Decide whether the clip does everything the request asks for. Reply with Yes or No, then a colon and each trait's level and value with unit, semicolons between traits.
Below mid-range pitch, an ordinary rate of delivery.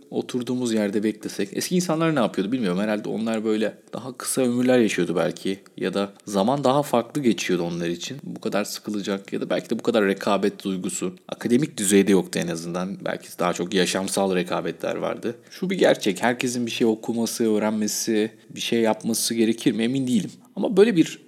No: low, 110 Hz; fast, 180 wpm